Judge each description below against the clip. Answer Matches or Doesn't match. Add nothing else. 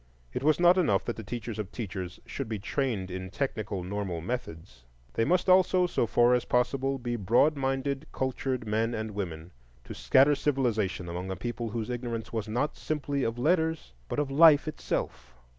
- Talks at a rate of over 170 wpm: Matches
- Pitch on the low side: Matches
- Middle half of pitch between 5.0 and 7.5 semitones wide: Matches